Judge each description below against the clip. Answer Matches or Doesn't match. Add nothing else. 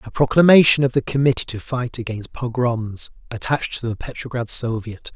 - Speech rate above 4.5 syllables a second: Matches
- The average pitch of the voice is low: Matches